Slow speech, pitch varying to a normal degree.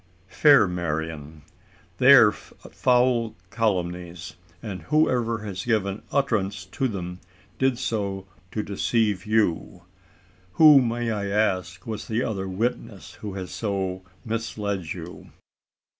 Yes: slow, 115 wpm; average, 3.8 semitones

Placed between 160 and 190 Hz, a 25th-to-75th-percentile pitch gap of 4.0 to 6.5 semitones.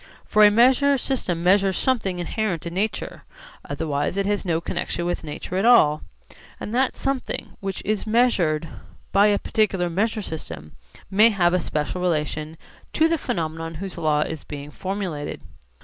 Yes: medium, 185 Hz; average, 4.8 semitones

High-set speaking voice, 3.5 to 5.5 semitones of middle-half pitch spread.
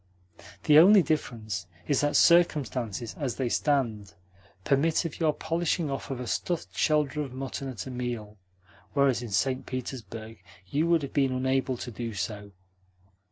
No: low, 130 Hz; average, 4.3 semitones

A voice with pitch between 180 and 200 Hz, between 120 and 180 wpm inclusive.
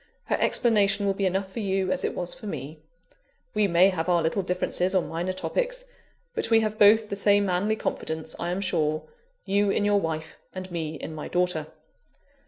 No: high, 190 Hz; average, 195 wpm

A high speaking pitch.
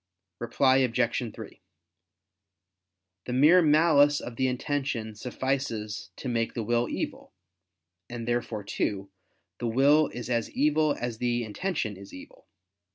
No: low, 120 Hz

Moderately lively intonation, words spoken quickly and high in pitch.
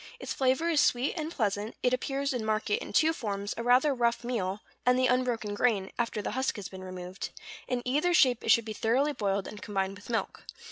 Yes: average, 4.2 semitones; fast, 220 wpm; high, 235 Hz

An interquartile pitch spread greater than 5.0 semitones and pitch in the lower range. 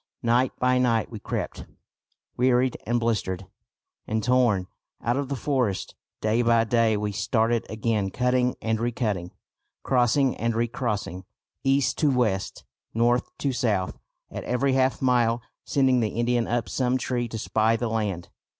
No: narrow, 2.4 semitones; low, 120 Hz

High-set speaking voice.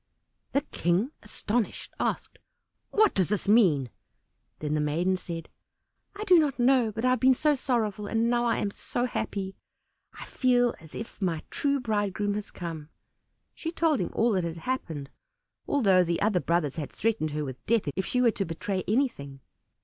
Yes: high, 210 Hz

